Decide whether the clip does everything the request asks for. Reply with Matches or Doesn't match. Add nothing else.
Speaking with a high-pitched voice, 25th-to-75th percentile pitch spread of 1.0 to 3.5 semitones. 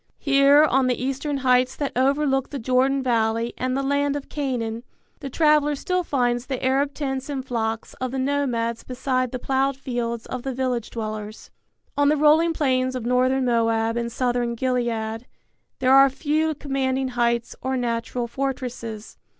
Matches